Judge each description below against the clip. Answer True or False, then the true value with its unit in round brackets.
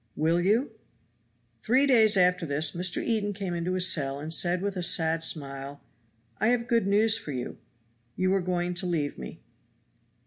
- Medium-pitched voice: True (180 Hz)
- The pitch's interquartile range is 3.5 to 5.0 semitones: True (4.1 semitones)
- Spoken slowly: False (175 wpm)